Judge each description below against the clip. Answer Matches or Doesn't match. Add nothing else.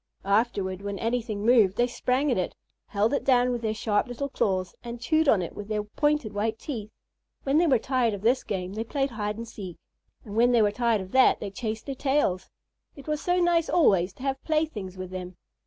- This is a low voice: Doesn't match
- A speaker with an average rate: Doesn't match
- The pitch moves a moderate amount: Matches